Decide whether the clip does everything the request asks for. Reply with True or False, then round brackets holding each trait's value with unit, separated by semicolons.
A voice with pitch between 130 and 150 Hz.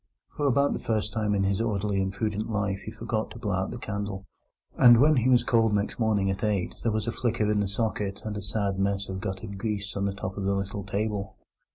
False (105 Hz)